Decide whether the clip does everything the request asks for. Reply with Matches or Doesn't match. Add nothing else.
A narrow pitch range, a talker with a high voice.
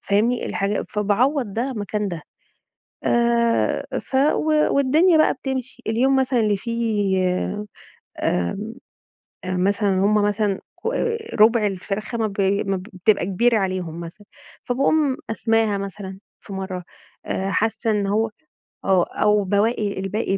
Doesn't match